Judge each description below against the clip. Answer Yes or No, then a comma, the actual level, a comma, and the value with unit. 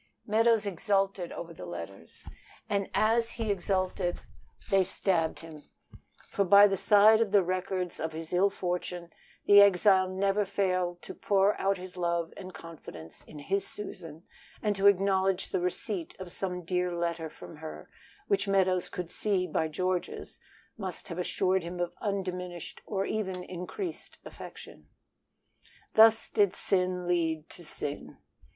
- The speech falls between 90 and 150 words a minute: Yes, average, 145 wpm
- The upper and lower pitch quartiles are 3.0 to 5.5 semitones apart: No, narrow, 2.4 semitones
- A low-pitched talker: No, medium, 185 Hz